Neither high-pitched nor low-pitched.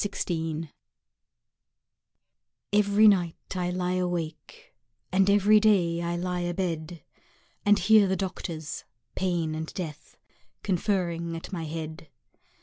Yes: medium, 175 Hz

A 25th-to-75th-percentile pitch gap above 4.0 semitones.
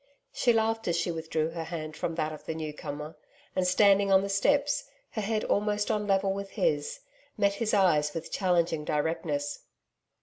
Yes: average, 4.5 semitones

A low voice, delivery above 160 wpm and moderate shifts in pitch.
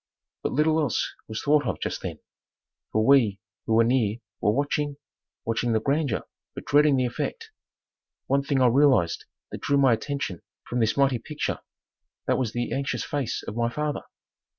Yes: low, 130 Hz; average, 175 wpm; average, 3.8 semitones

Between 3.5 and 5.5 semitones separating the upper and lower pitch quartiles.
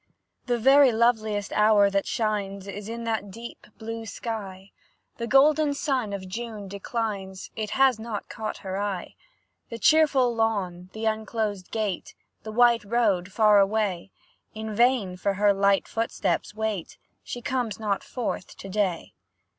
No: average, 2.8 semitones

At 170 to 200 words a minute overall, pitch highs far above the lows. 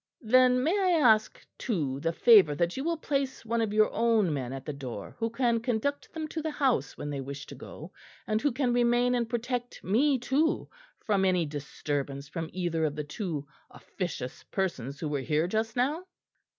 Yes: average, 195 wpm; wide, 8.8 semitones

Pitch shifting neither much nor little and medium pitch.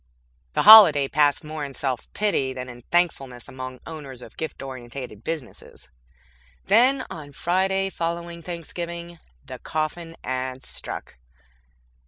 Yes: average, 4.8 semitones; medium, 155 Hz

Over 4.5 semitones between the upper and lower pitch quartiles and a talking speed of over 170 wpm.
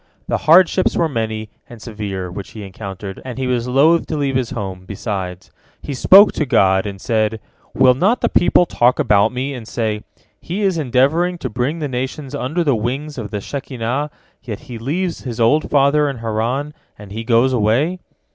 Yes: average, 5.2 semitones; average, 190 wpm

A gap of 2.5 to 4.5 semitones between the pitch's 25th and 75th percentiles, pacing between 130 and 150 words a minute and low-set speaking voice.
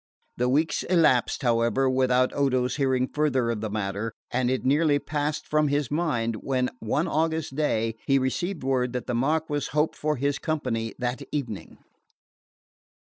No: average, 3.4 semitones; average, 160 wpm; low, 130 Hz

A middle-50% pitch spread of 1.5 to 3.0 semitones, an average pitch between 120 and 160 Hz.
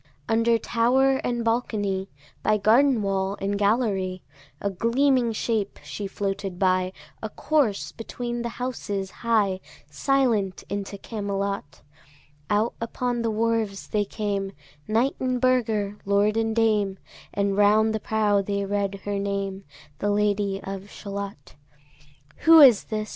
No: narrow, 2.6 semitones; high, 210 Hz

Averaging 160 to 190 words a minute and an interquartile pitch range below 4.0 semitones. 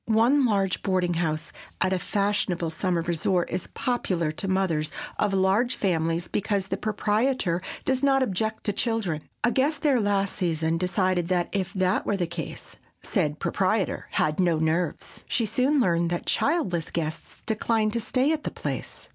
No: average, 165 wpm; average, 4.4 semitones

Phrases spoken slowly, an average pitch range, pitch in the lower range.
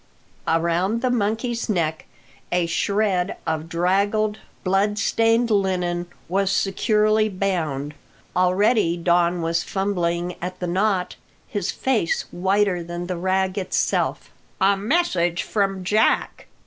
No: slow, 115 wpm; average, 3.2 semitones; high, 190 Hz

